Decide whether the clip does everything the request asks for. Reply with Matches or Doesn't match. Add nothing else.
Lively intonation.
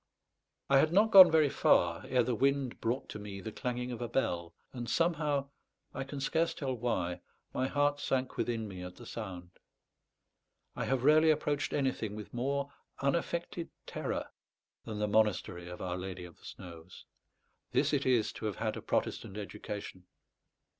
Matches